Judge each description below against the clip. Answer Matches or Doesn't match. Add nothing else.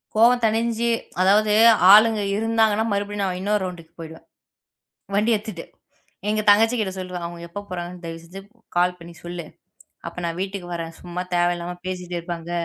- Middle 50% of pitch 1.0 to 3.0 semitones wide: Doesn't match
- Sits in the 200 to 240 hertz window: Doesn't match